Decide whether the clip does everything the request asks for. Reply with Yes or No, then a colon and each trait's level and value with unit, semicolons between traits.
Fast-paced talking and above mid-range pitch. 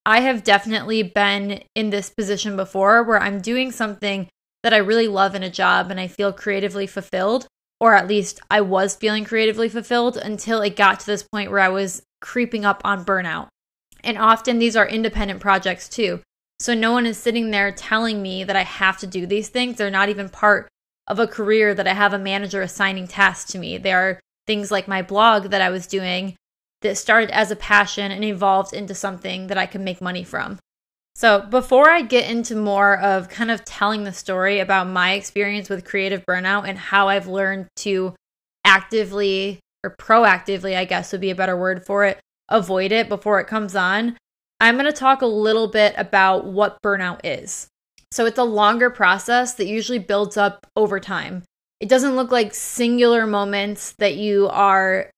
No: average, 195 wpm; high, 200 Hz